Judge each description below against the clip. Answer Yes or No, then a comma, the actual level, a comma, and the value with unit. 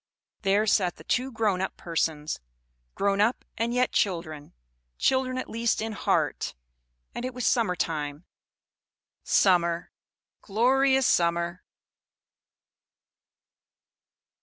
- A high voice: Yes, high, 200 Hz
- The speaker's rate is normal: No, slow, 105 wpm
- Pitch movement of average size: No, wide, 5.9 semitones